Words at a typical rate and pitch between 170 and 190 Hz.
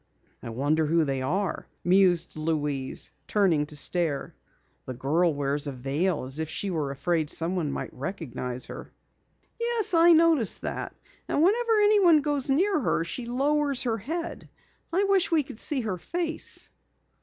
Yes: average, 155 wpm; medium, 185 Hz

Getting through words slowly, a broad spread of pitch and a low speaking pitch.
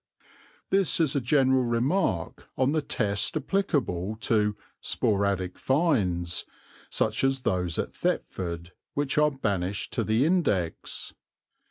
Yes: slow, 120 wpm; wide, 7.3 semitones; low, 115 Hz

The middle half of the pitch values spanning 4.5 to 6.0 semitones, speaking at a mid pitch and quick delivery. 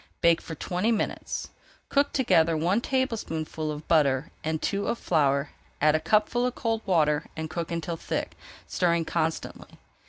No: average, 5.2 semitones; medium, 165 Hz; average, 155 wpm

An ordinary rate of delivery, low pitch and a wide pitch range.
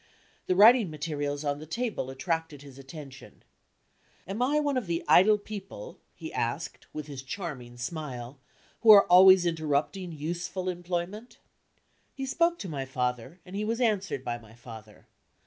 No: average, 155 wpm; medium, 165 Hz; wide, 6.4 semitones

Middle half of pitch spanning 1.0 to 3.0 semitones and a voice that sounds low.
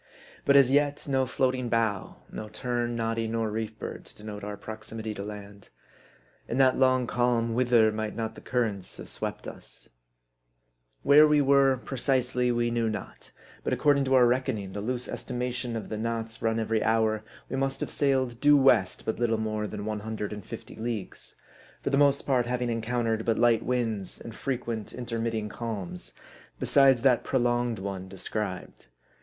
Yes: average, 2.7 semitones; low, 115 Hz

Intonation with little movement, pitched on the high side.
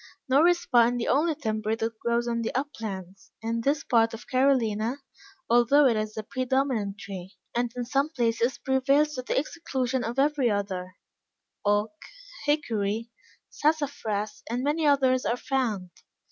No: average, 4.0 semitones; high, 240 Hz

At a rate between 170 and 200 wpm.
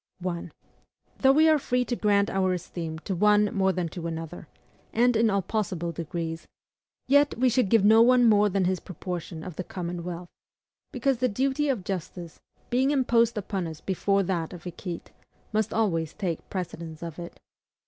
Yes: average, 180 wpm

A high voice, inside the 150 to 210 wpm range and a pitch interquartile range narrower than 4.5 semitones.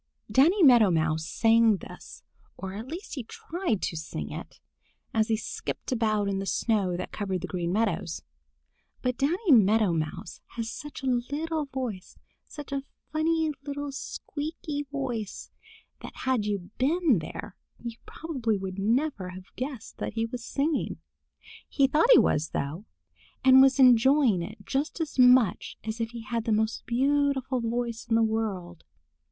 No: high, 235 Hz; average, 160 wpm; wide, 5.4 semitones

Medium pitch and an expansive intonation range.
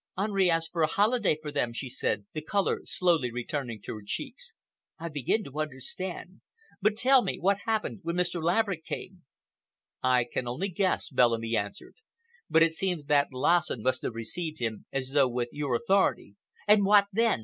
Yes: medium, 160 Hz; wide, 7.0 semitones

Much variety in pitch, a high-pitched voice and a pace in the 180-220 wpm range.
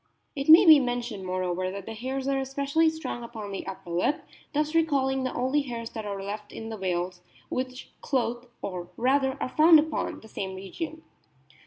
Yes: wide, 5.9 semitones; high, 245 Hz; average, 185 wpm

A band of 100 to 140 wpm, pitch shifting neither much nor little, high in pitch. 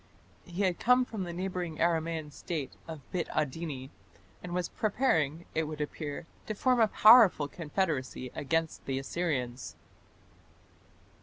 No: slow, 135 wpm; average, 3.8 semitones; medium, 165 Hz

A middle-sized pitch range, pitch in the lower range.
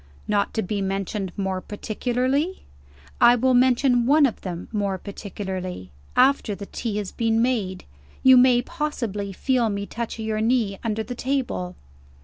No: average, 4.1 semitones; high, 220 Hz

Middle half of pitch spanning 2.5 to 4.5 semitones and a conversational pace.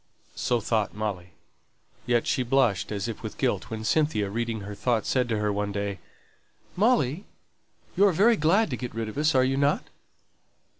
No: average, 5.3 semitones; average, 180 wpm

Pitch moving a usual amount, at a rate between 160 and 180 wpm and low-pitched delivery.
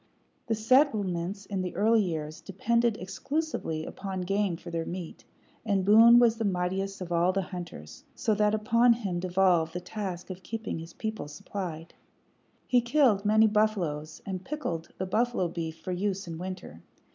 No: average, 3.9 semitones; average, 165 wpm; high, 195 Hz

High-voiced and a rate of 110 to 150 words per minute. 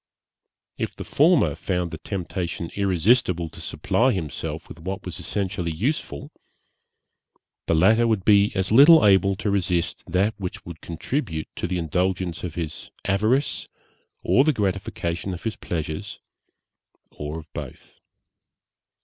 No: very low, 95 Hz; slow, 135 wpm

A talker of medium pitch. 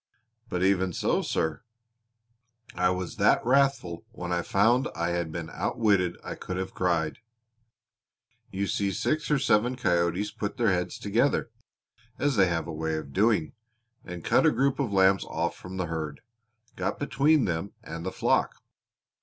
No: very low, 95 Hz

